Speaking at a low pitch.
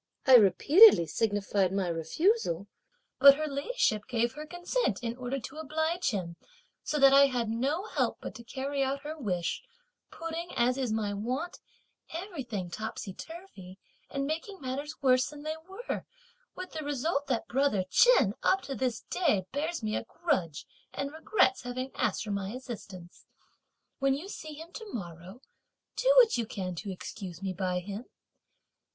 No: very high, 260 Hz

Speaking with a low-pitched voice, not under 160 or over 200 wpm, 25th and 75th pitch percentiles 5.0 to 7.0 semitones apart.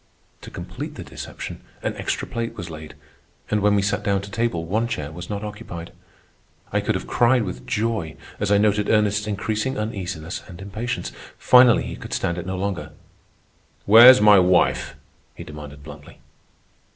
No: low, 100 Hz; average, 170 wpm; average, 3.6 semitones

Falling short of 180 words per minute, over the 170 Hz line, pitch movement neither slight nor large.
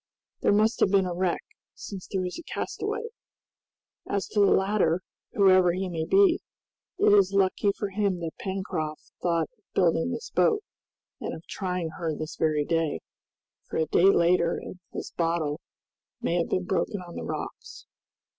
Yes: average, 170 wpm; medium, 185 Hz; average, 3.0 semitones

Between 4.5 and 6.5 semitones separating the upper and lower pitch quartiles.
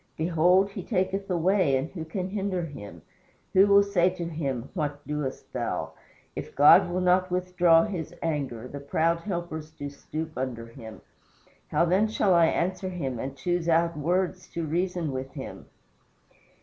No: average, 4.1 semitones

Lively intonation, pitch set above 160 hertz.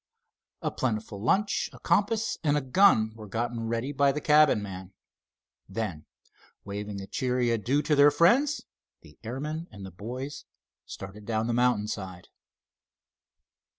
No: wide, 5.8 semitones; low, 120 Hz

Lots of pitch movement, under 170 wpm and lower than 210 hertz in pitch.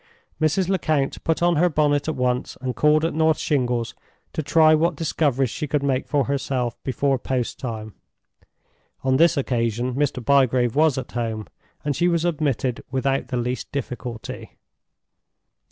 No: average, 3.7 semitones; average, 155 wpm; low, 135 Hz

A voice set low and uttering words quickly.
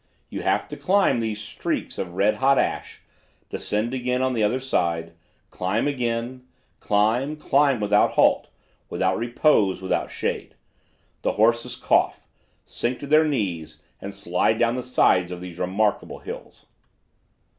No: low, 115 Hz; average, 145 wpm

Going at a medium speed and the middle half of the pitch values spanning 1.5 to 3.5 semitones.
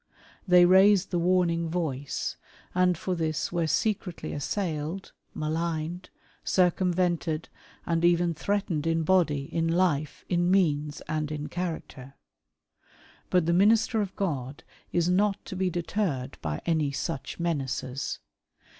No: slow, 125 wpm; average, 3.1 semitones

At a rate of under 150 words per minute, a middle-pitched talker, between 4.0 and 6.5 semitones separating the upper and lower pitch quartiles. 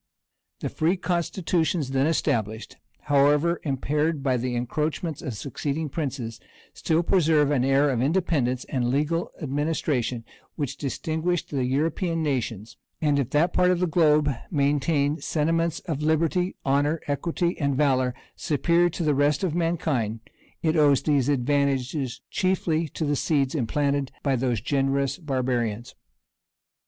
No: slow, 135 wpm; medium, 145 Hz; average, 3.4 semitones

